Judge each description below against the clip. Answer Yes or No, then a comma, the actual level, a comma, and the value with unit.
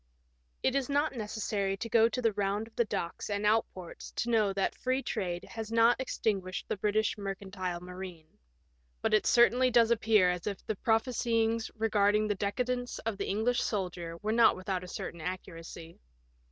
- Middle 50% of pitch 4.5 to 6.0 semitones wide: No, average, 3.3 semitones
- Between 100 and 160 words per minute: No, average, 175 wpm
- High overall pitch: Yes, high, 210 Hz